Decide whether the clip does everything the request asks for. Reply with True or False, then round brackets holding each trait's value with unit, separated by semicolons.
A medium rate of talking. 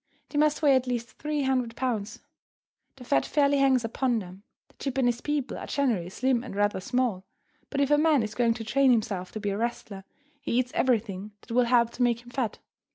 False (215 wpm)